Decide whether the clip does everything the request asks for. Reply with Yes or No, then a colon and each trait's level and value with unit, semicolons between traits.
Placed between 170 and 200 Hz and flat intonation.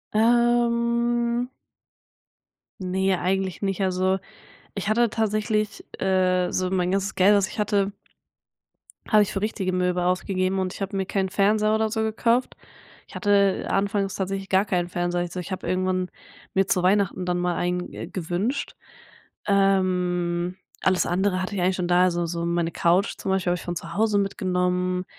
Yes: high, 190 Hz; narrow, 2.1 semitones